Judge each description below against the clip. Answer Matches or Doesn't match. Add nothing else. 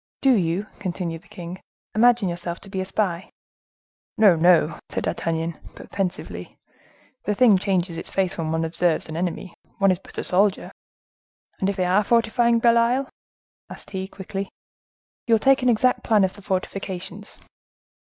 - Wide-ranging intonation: Doesn't match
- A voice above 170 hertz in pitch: Matches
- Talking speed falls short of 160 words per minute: Doesn't match